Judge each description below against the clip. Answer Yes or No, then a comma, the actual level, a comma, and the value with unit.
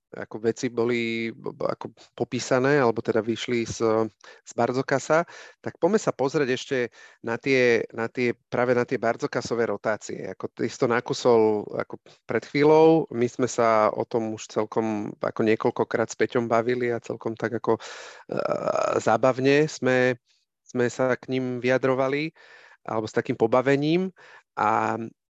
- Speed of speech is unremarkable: Yes, average, 150 wpm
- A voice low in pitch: Yes, low, 120 Hz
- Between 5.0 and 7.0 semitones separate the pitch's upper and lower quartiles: No, narrow, 2.4 semitones